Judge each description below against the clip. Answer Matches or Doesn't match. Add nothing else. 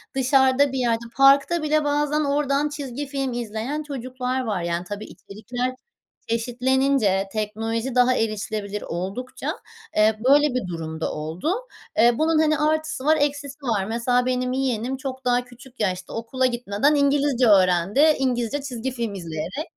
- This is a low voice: Doesn't match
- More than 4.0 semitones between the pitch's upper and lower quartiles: Matches